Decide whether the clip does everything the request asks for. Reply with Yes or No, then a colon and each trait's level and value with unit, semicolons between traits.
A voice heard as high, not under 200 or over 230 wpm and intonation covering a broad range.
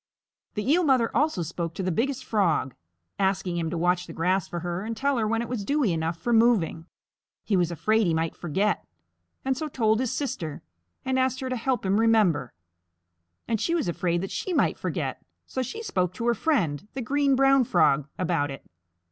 Yes: high, 210 Hz; fast, 205 wpm; wide, 6.9 semitones